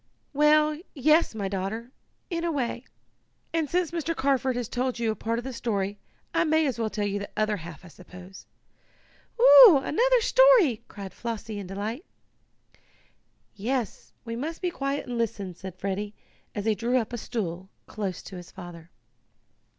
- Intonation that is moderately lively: No, wide, 6.8 semitones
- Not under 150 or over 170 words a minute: Yes, average, 165 wpm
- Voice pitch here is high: Yes, high, 230 Hz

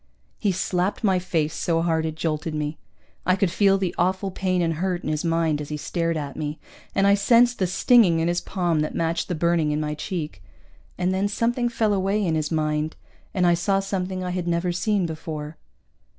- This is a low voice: No, medium, 175 Hz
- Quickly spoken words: Yes, fast, 210 wpm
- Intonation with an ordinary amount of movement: Yes, average, 3.3 semitones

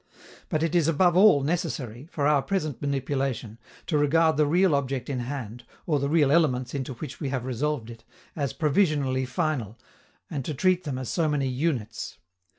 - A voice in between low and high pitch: Yes, medium, 145 Hz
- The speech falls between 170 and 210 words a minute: Yes, average, 180 wpm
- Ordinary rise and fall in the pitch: Yes, average, 3.4 semitones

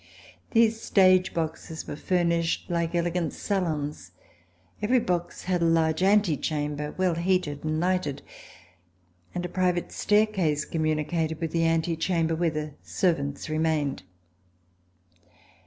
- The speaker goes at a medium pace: No, slow, 120 wpm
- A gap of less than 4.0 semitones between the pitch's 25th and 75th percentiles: Yes, average, 2.7 semitones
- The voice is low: No, medium, 165 Hz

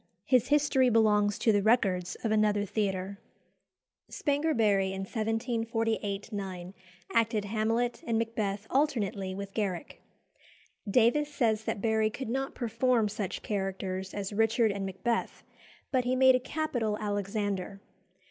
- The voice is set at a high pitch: Yes, high, 215 Hz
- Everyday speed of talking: No, slow, 130 wpm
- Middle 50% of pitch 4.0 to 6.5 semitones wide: No, average, 3.0 semitones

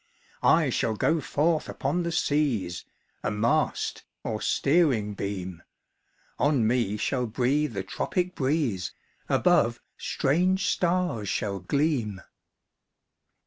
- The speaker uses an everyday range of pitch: No, wide, 6.9 semitones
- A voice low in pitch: Yes, low, 130 Hz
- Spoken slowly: Yes, slow, 105 wpm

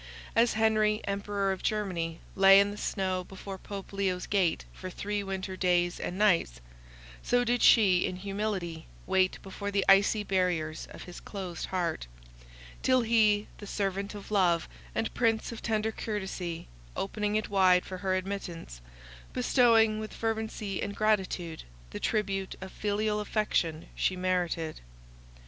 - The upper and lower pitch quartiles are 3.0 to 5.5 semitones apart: No, narrow, 2.5 semitones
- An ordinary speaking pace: Yes, average, 145 wpm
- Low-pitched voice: No, high, 195 Hz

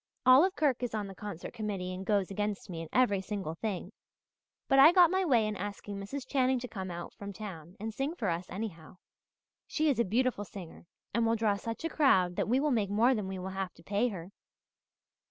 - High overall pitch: Yes, high, 210 Hz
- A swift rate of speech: Yes, fast, 225 wpm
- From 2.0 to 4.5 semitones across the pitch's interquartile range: No, average, 4.9 semitones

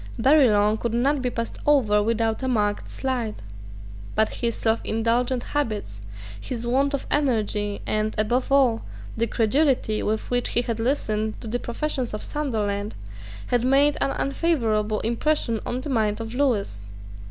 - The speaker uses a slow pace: No, average, 150 wpm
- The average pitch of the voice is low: No, high, 230 Hz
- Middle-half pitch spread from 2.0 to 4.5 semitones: Yes, average, 3.5 semitones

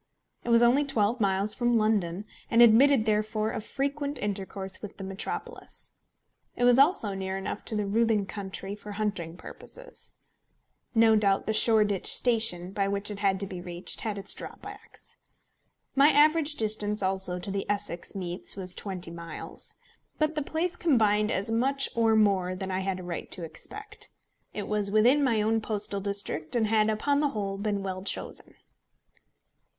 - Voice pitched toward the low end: No, high, 210 Hz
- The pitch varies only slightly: No, average, 3.2 semitones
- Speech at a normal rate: Yes, average, 170 wpm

